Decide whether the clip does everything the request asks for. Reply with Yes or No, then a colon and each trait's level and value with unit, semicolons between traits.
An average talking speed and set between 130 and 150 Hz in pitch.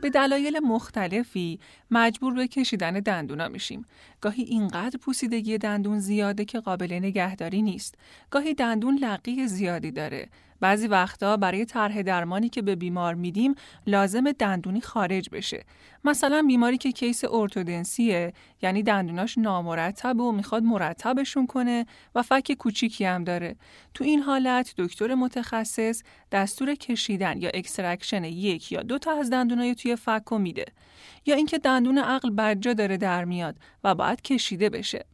No: average, 140 wpm; high, 225 Hz